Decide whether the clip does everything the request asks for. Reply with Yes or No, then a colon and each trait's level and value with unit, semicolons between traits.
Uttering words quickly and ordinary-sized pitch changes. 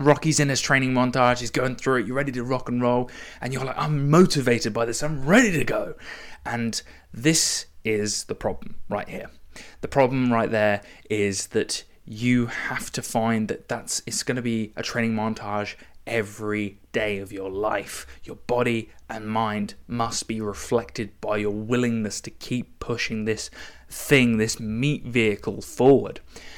No: average, 170 wpm; average, 3.2 semitones